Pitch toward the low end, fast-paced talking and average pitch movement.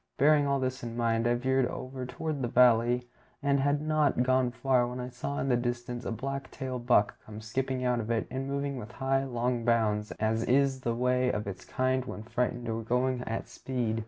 No: low, 125 Hz; fast, 215 wpm; narrow, 2.0 semitones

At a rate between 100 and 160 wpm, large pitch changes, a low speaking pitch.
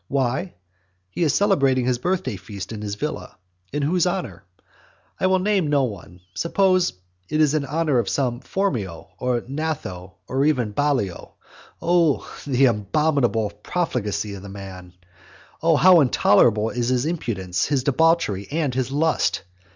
Yes: average, 150 wpm; wide, 7.2 semitones; low, 130 Hz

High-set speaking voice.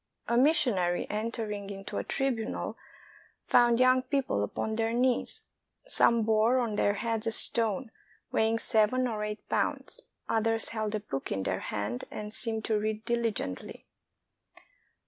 Yes: high, 225 Hz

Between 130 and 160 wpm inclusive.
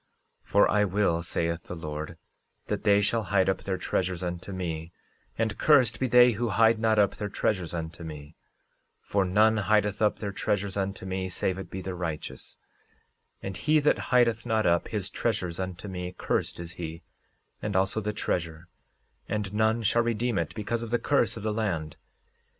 No: average, 185 wpm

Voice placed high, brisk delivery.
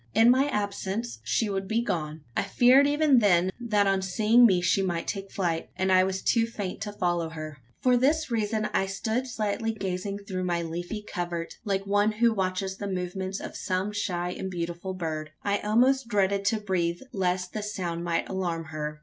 No: high, 195 Hz; average, 190 wpm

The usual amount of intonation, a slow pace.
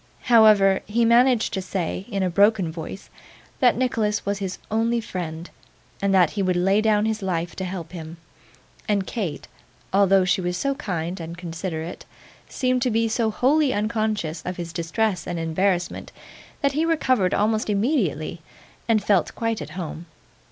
No: average, 4.0 semitones; average, 165 wpm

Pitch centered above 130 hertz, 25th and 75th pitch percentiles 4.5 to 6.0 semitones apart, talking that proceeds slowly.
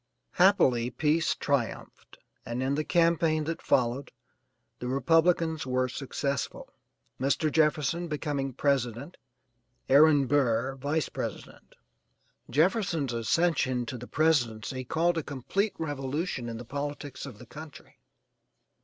No: medium, 140 Hz; average, 3.9 semitones; slow, 115 wpm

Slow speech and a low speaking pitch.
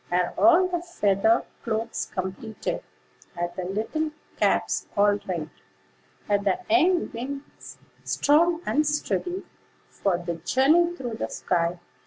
No: slow, 125 wpm; high, 230 Hz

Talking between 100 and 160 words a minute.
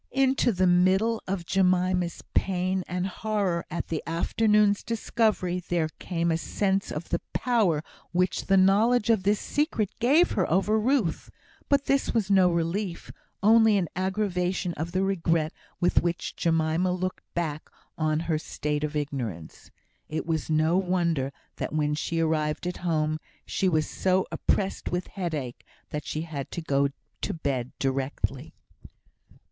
Yes: average, 150 wpm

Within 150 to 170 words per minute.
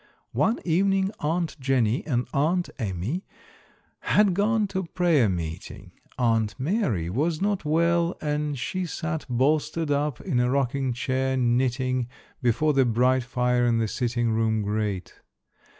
No: slow, 135 wpm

